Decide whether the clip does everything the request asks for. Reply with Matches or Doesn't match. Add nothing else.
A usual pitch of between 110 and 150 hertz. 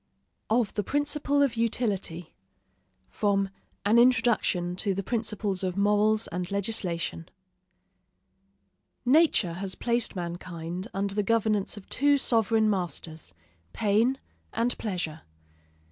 Doesn't match